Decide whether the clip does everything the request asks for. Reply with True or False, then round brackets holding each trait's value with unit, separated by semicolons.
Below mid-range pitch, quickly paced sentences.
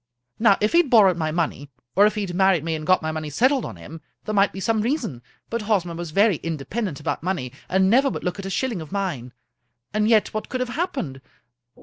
False (195 Hz; 240 wpm)